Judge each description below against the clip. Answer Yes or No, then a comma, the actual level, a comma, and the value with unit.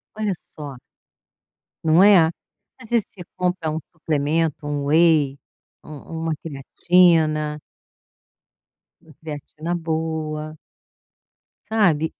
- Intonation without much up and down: Yes, narrow, 2.2 semitones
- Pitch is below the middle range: No, medium, 160 Hz